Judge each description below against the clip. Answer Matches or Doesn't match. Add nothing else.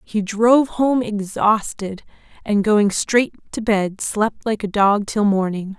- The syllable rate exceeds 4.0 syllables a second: Doesn't match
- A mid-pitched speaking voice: Doesn't match